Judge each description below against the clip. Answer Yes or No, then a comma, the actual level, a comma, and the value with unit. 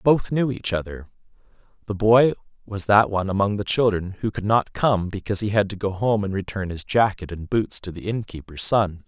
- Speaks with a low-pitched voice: Yes, low, 100 Hz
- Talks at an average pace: No, fast, 210 wpm